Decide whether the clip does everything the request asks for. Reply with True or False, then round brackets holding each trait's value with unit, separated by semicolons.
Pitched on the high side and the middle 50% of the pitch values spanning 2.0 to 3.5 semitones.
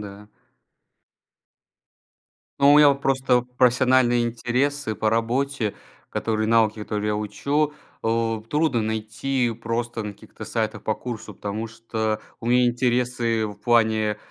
False (115 Hz; 2.5 semitones)